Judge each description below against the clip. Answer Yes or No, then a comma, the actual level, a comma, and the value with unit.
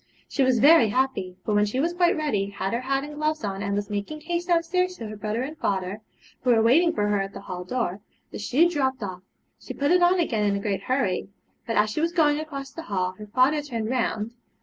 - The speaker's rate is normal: No, fast, 245 wpm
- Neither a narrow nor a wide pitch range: No, wide, 6.9 semitones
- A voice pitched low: No, very high, 250 Hz